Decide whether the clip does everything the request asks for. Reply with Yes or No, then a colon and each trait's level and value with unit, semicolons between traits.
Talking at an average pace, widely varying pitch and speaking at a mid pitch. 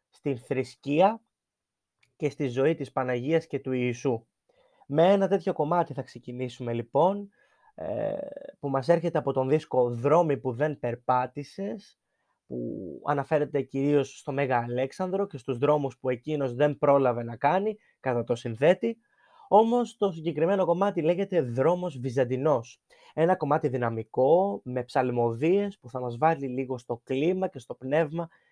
Yes: average, 140 wpm; wide, 6.0 semitones; medium, 145 Hz